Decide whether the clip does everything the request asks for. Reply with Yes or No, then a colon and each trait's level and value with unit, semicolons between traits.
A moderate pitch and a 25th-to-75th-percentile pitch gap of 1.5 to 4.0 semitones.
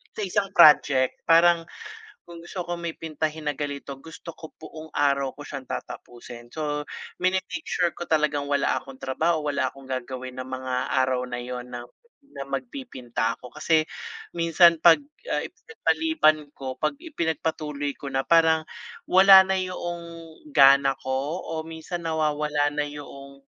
Yes: medium, 150 Hz; average, 3.7 semitones